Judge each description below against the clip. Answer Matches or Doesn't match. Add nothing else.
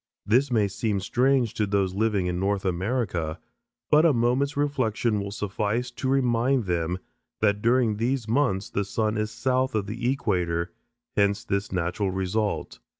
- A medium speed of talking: Matches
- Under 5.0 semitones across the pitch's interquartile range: Matches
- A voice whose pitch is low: Matches